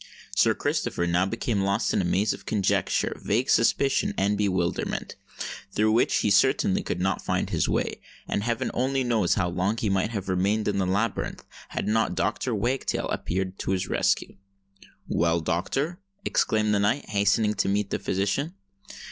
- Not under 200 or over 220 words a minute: No, average, 170 wpm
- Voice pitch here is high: No, low, 100 Hz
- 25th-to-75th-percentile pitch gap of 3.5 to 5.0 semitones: No, average, 3.1 semitones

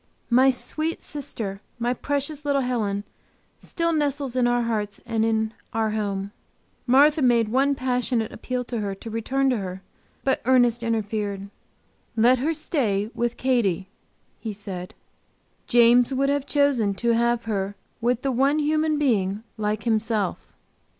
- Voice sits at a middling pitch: No, high, 235 Hz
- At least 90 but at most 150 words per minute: Yes, average, 145 wpm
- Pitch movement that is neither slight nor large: Yes, average, 4.0 semitones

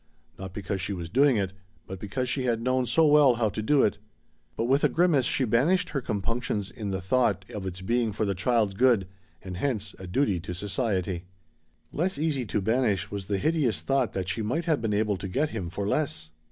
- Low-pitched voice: Yes, low, 110 Hz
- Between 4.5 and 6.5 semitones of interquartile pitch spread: Yes, average, 5.2 semitones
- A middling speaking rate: No, fast, 220 wpm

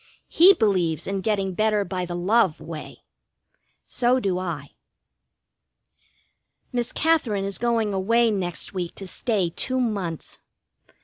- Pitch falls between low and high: No, high, 200 Hz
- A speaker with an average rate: No, slow, 125 wpm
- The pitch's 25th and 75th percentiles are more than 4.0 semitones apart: Yes, average, 4.4 semitones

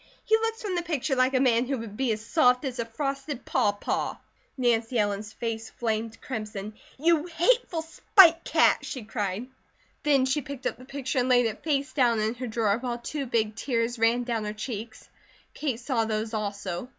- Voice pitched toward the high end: Yes, high, 245 Hz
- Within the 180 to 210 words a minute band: Yes, average, 190 wpm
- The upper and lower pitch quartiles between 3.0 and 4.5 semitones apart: Yes, average, 3.8 semitones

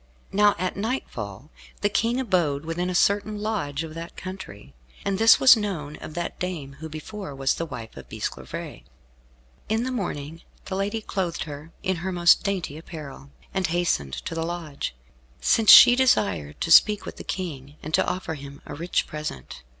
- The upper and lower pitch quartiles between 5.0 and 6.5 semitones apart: Yes, wide, 5.5 semitones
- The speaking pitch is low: No, medium, 170 Hz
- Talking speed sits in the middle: Yes, average, 180 wpm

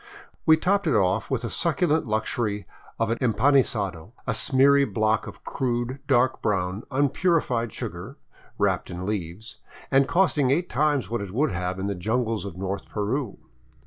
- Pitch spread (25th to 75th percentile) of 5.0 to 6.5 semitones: Yes, wide, 5.5 semitones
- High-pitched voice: No, low, 115 Hz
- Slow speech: No, average, 160 wpm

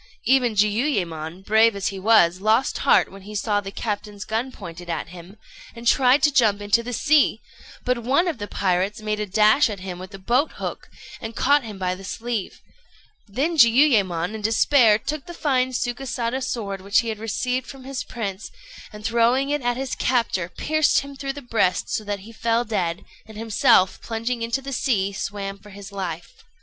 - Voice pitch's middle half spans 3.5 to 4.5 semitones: Yes, average, 4.1 semitones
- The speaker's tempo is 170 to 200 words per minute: Yes, average, 195 wpm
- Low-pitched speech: No, high, 220 Hz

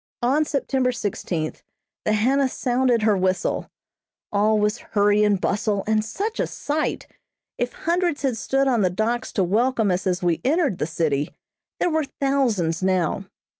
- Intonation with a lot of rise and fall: Yes, wide, 5.7 semitones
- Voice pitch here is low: No, high, 220 Hz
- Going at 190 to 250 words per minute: No, average, 160 wpm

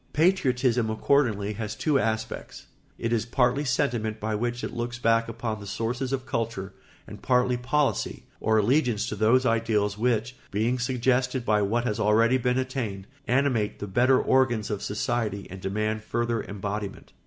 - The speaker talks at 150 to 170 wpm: Yes, average, 160 wpm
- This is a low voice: Yes, low, 115 Hz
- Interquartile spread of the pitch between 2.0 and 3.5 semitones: Yes, average, 2.8 semitones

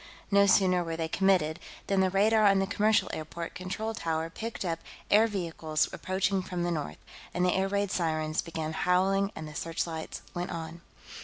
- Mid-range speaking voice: Yes, medium, 180 Hz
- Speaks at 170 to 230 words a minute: Yes, average, 180 wpm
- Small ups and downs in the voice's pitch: No, average, 3.2 semitones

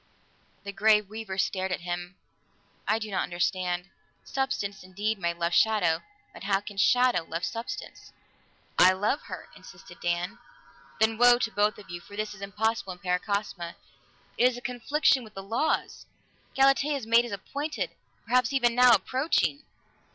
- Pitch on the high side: Yes, high, 210 Hz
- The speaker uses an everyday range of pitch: Yes, average, 4.5 semitones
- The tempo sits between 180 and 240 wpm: No, average, 160 wpm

